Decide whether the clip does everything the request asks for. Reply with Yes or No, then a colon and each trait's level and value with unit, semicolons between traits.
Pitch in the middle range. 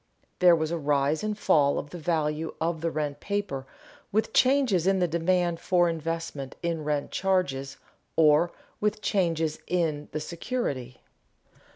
Yes: medium, 165 Hz